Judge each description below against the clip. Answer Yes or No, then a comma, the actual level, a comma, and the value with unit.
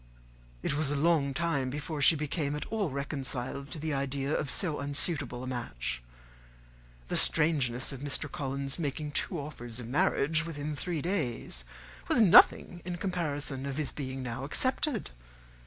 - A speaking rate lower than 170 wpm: Yes, average, 155 wpm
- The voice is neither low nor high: Yes, medium, 145 Hz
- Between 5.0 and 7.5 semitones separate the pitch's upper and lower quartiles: No, average, 3.0 semitones